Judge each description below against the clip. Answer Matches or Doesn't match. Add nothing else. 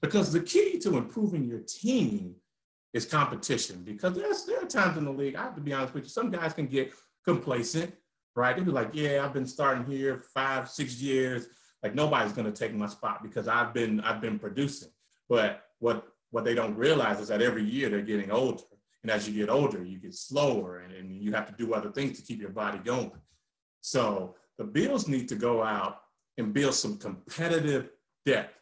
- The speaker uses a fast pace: Matches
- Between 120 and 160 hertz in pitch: Matches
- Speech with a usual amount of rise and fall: Doesn't match